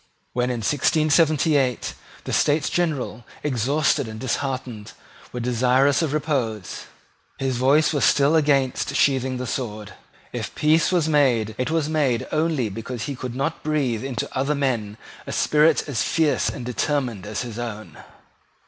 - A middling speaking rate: Yes, average, 150 wpm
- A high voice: No, low, 135 Hz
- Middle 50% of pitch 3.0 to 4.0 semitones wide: Yes, average, 3.7 semitones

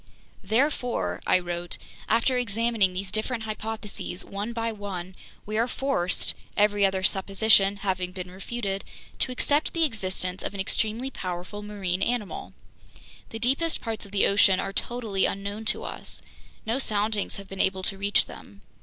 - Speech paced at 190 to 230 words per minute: No, average, 155 wpm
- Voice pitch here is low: No, high, 205 Hz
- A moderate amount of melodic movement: Yes, average, 3.1 semitones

